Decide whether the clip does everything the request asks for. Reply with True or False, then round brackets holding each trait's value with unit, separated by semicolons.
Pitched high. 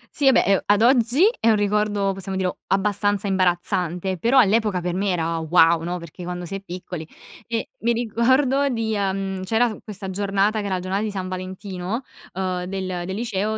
True (195 Hz)